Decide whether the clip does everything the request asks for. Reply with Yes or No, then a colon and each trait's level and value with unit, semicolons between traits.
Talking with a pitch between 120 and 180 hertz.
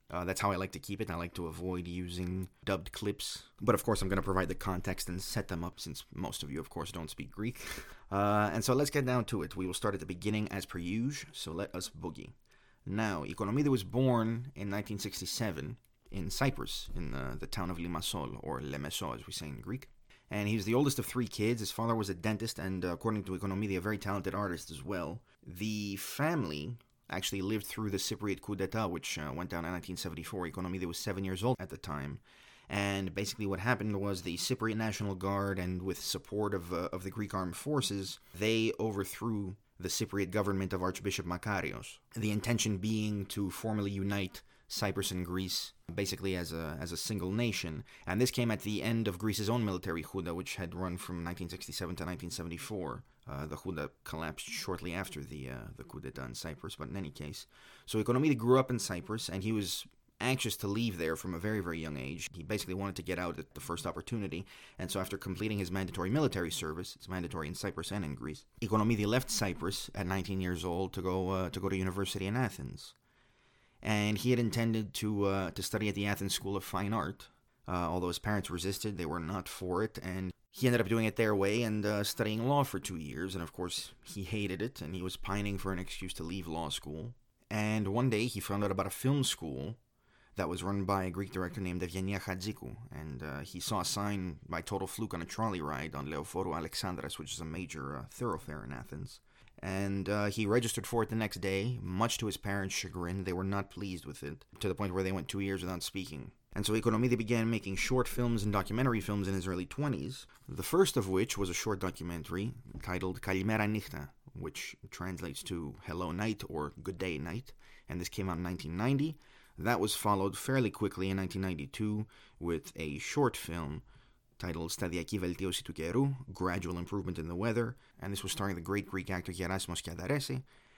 No: very low, 95 Hz